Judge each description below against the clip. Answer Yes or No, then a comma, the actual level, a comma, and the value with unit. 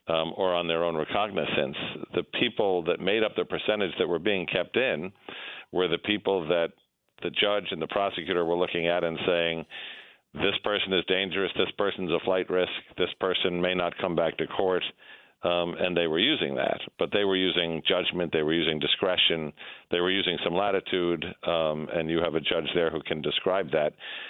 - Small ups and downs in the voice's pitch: Yes, narrow, 1.9 semitones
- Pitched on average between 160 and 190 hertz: No, very low, 85 Hz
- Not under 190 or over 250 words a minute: Yes, average, 200 wpm